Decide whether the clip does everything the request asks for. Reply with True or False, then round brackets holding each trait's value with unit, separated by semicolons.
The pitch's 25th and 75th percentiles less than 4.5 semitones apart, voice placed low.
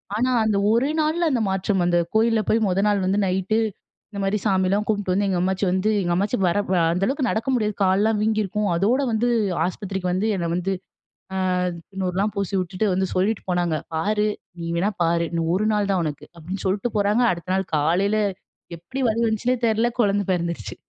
False (2.9 semitones; 195 Hz)